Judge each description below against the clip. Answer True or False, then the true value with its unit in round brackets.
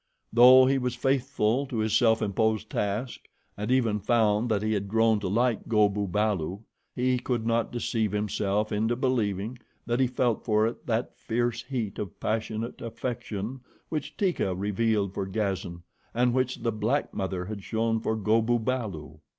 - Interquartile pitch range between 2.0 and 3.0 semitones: True (2.7 semitones)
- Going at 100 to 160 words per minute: False (170 wpm)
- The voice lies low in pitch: True (110 Hz)